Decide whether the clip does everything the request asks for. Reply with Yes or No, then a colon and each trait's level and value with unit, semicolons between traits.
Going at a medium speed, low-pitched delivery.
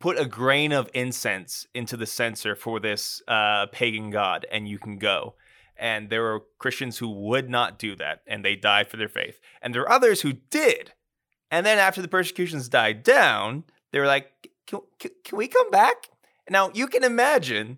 Yes: average, 195 wpm; low, 130 Hz